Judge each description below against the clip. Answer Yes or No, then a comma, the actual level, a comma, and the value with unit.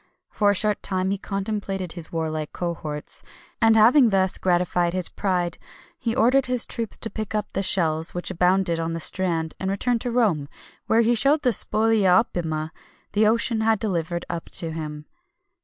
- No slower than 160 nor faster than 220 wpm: Yes, average, 175 wpm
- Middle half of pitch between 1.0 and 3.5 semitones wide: No, average, 4.7 semitones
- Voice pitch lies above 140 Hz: Yes, high, 190 Hz